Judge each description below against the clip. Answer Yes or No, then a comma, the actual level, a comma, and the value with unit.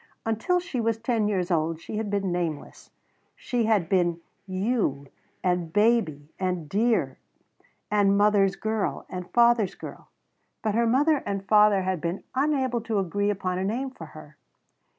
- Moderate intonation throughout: Yes, average, 4.1 semitones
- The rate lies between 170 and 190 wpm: No, average, 155 wpm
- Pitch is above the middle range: Yes, high, 205 Hz